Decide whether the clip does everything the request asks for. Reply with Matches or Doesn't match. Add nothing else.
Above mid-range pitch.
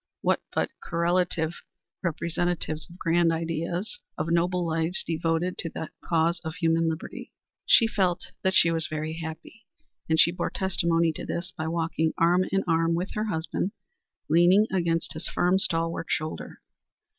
Doesn't match